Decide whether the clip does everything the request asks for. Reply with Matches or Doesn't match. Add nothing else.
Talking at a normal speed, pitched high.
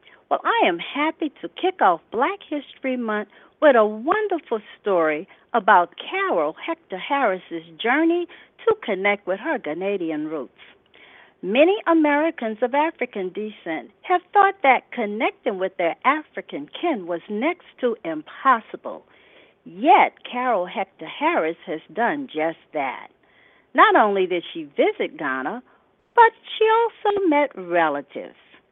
Doesn't match